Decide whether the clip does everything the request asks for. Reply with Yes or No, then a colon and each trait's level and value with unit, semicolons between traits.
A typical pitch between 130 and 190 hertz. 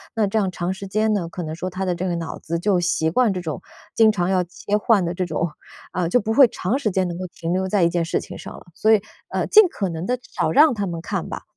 Yes: medium, 185 Hz